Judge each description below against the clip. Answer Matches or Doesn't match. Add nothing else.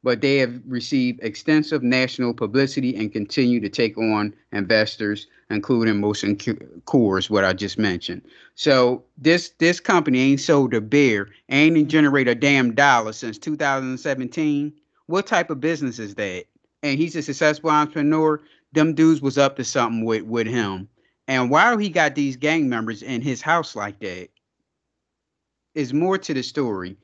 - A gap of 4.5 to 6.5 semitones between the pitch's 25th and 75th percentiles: Matches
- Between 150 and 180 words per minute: Matches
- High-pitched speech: Doesn't match